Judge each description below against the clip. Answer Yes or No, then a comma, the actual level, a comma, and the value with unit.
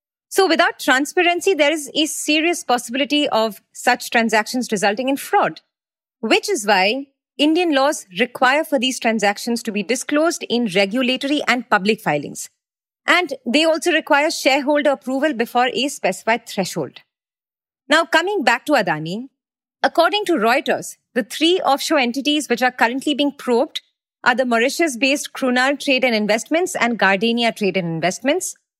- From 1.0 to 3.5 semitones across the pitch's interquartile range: No, average, 4.6 semitones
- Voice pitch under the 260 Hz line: No, very high, 265 Hz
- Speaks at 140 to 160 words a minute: Yes, average, 150 wpm